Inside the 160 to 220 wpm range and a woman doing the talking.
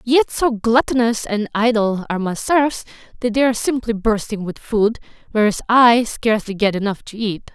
Yes: average, 175 wpm; female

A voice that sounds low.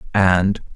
Yes: very low, 95 Hz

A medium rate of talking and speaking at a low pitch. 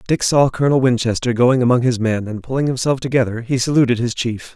No: fast, 210 wpm; low, 125 Hz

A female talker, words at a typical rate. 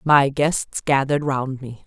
Yes: female; average, 160 wpm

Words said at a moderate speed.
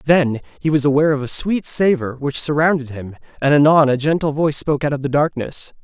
No: fast, 215 wpm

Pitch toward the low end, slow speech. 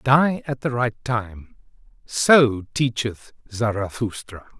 Yes: low, 120 Hz; slow, 105 wpm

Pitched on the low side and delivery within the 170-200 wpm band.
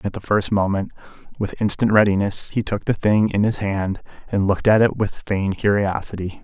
Yes: low, 100 Hz; average, 195 wpm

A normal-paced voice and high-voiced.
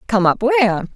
Yes: average, 190 wpm; high, 225 Hz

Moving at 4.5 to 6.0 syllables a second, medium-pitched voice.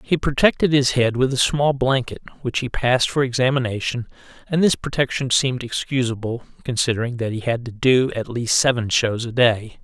No: 5.4 syllables/s; low, 125 Hz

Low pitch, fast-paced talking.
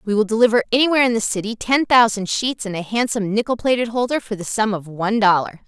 No: high, 220 Hz; fast, 230 wpm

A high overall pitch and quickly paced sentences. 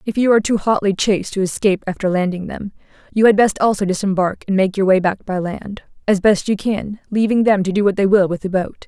Yes: high, 200 Hz; fast, 250 wpm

